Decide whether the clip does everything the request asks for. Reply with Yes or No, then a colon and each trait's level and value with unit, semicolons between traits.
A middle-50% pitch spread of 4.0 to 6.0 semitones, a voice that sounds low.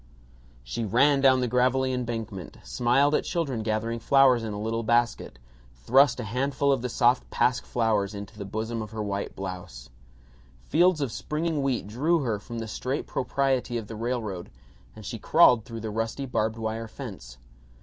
No: average, 3.4 semitones; low, 115 Hz